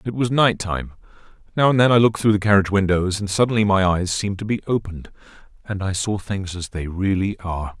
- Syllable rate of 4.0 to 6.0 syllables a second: No, 6.2 syllables/s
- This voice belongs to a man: Yes, male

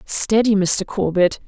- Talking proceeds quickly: No, slow, 120 wpm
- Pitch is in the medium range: No, high, 195 Hz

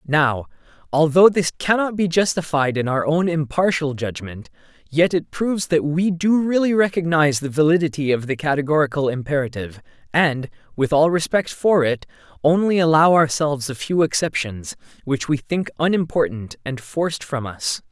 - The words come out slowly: No, average, 150 wpm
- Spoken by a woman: No, male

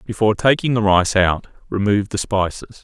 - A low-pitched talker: Yes, low, 105 Hz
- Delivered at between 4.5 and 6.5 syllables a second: Yes, 5.5 syllables/s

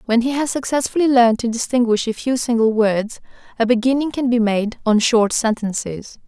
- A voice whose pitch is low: No, high, 235 Hz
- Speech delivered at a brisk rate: No, average, 180 wpm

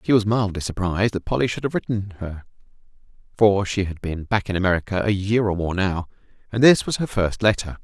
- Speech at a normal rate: No, fast, 215 wpm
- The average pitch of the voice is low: Yes, low, 100 Hz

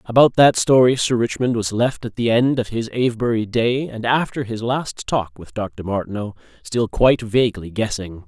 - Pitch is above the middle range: No, low, 115 Hz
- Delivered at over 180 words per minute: Yes, average, 190 wpm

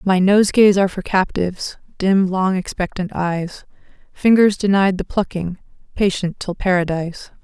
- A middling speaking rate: No, slow, 130 wpm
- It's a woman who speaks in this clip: Yes, female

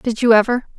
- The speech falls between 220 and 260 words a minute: Yes, fast, 230 wpm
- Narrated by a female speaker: Yes, female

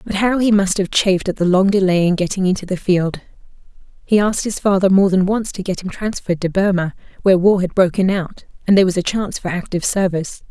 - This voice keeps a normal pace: No, fast, 235 wpm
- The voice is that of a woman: Yes, female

